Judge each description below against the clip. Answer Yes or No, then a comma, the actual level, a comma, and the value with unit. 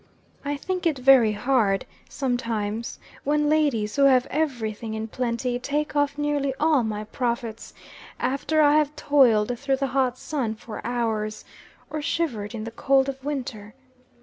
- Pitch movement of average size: Yes, average, 4.4 semitones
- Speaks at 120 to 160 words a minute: Yes, average, 155 wpm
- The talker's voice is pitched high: Yes, very high, 255 Hz